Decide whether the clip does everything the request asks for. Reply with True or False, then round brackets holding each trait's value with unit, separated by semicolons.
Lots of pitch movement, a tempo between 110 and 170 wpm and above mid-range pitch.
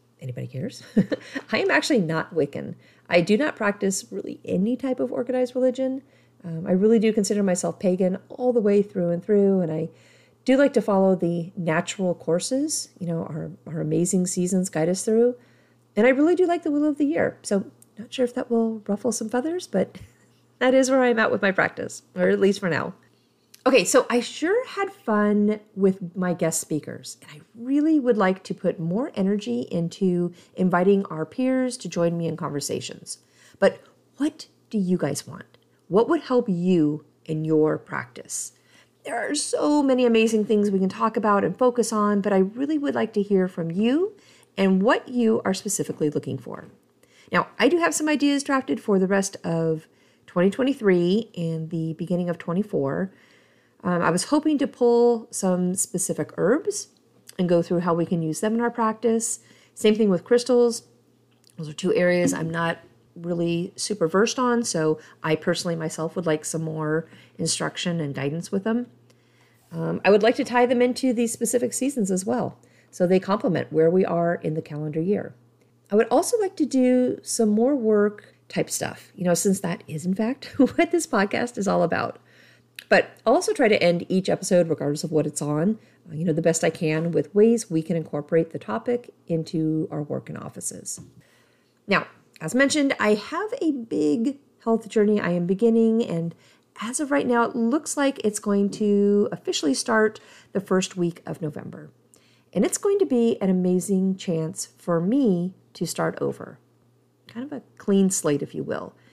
False (6.1 semitones; 190 wpm; 200 Hz)